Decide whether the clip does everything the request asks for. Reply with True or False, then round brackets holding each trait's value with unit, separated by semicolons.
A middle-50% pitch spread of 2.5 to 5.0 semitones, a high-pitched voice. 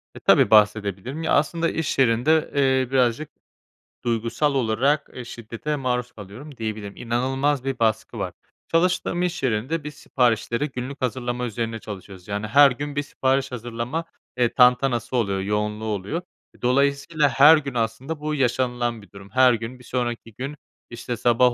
False (3.7 semitones; 125 Hz)